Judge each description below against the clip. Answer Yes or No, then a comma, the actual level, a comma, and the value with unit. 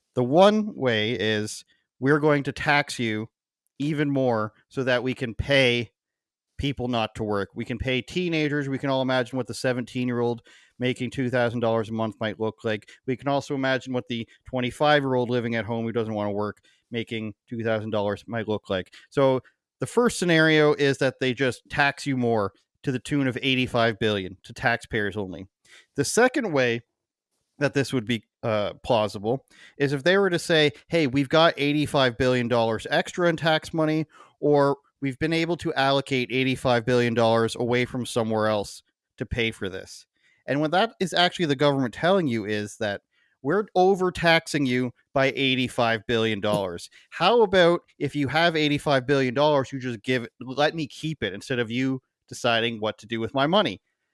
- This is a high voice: No, low, 130 Hz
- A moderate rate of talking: Yes, average, 175 wpm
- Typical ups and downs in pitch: Yes, average, 4.2 semitones